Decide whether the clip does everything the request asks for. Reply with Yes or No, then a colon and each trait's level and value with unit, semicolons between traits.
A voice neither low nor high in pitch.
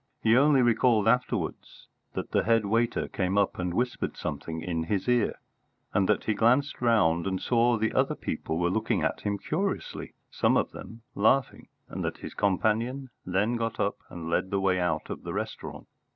No: low, 110 Hz